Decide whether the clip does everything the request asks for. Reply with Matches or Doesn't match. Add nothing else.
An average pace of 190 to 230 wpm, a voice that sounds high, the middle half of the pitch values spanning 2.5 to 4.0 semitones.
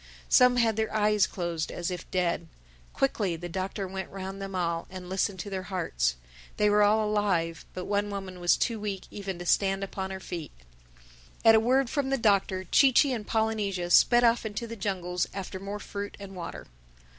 Matches